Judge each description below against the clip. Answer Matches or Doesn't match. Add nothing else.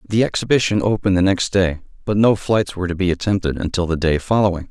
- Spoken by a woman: Doesn't match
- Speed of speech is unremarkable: Doesn't match